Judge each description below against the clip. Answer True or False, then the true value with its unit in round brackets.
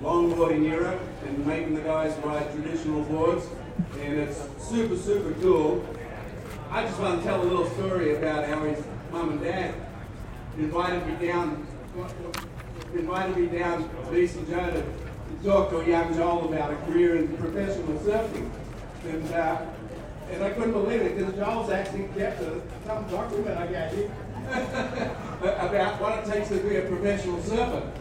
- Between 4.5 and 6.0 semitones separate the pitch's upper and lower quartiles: False (3.7 semitones)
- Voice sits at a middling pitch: True (170 Hz)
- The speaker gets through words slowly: False (160 wpm)